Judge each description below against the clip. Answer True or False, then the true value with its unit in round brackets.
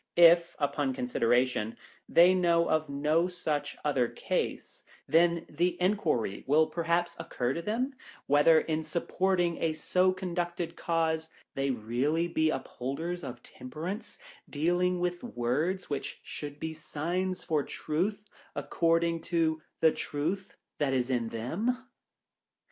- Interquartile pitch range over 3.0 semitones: True (3.5 semitones)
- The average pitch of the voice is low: False (165 Hz)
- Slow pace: True (130 wpm)